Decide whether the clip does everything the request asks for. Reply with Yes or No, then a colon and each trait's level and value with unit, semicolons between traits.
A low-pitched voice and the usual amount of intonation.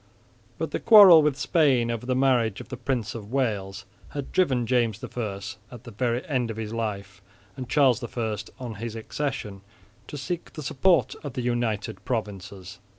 Yes: low, 120 Hz; average, 3.7 semitones